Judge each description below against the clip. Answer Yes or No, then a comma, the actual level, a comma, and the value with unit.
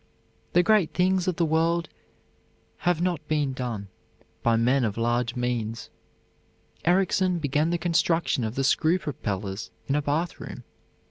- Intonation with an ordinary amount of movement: No, wide, 6.2 semitones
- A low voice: No, medium, 150 Hz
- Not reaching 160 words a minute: Yes, average, 140 wpm